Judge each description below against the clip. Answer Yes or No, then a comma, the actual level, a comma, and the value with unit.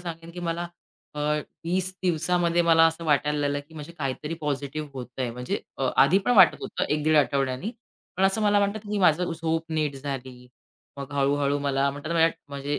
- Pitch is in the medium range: Yes, medium, 150 Hz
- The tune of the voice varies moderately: Yes, average, 3.3 semitones